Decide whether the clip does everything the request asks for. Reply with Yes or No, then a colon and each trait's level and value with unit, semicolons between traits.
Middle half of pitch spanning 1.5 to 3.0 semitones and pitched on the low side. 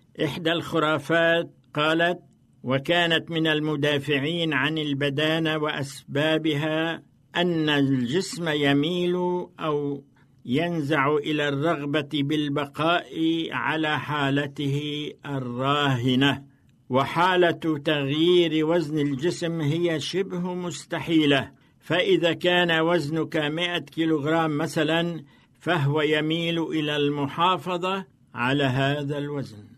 No: average, 2.7 semitones; medium, 155 Hz